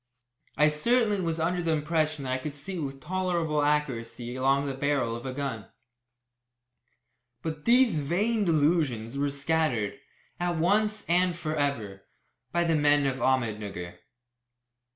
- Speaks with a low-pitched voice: No, medium, 150 Hz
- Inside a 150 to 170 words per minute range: No, average, 140 wpm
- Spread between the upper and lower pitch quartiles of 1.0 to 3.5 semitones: No, average, 4.3 semitones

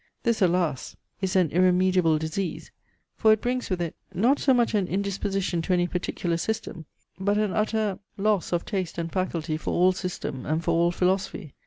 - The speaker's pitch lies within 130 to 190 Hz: Yes, medium, 185 Hz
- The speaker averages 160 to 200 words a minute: Yes, average, 180 wpm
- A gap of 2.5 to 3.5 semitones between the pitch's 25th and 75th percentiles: Yes, average, 3.0 semitones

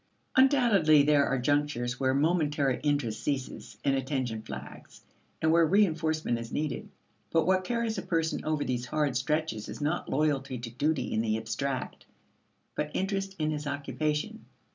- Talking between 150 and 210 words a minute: Yes, average, 155 wpm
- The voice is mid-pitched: Yes, medium, 150 Hz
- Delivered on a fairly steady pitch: No, average, 3.7 semitones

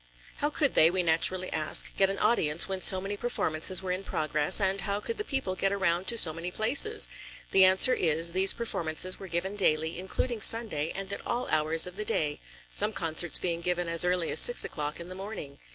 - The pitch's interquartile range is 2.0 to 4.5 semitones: Yes, average, 3.4 semitones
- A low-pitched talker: No, medium, 185 Hz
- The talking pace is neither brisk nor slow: No, fast, 215 wpm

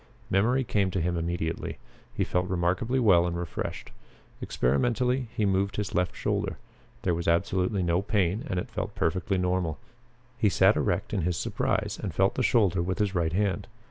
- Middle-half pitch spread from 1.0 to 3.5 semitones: Yes, average, 3.0 semitones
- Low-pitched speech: Yes, very low, 95 Hz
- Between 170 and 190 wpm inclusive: Yes, average, 175 wpm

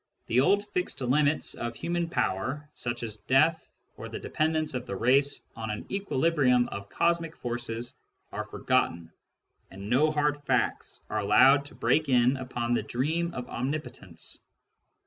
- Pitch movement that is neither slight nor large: Yes, average, 4.6 semitones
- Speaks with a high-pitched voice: No, low, 130 Hz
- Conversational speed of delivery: Yes, average, 155 wpm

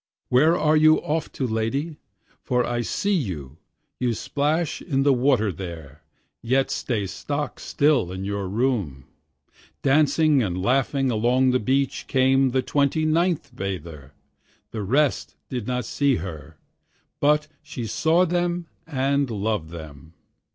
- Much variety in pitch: Yes, wide, 6.7 semitones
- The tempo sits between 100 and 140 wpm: Yes, slow, 135 wpm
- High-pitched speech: No, low, 130 Hz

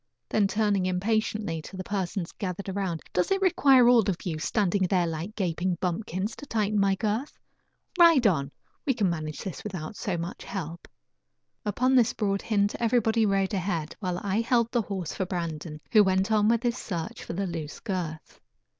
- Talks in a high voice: Yes, high, 195 Hz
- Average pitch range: Yes, average, 3.8 semitones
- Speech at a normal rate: Yes, average, 180 wpm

